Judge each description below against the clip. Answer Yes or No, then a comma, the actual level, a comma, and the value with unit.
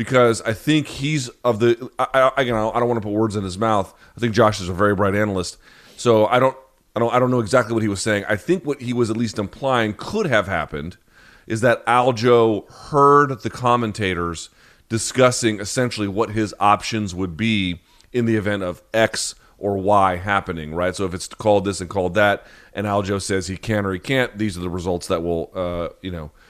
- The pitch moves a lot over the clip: No, average, 3.9 semitones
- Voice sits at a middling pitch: No, low, 110 Hz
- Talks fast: Yes, fast, 220 wpm